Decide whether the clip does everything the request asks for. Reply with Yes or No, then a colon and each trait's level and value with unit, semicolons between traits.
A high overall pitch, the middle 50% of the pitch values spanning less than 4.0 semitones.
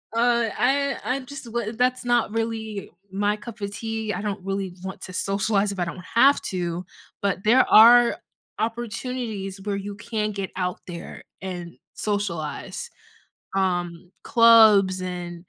Yes: high, 205 Hz; average, 3.5 semitones